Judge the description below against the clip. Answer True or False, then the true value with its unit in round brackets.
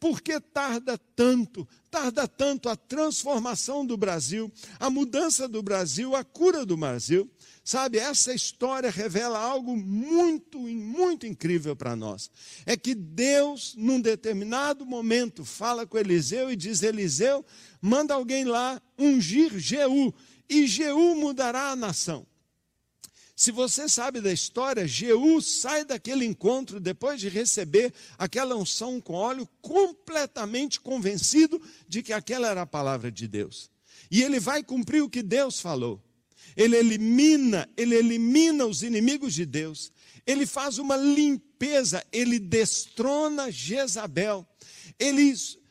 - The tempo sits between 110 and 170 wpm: True (130 wpm)